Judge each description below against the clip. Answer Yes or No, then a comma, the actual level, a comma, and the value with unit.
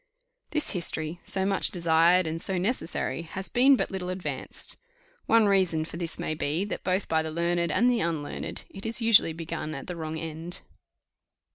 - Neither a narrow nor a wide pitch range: Yes, average, 3.3 semitones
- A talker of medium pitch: Yes, medium, 175 Hz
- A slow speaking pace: No, average, 180 wpm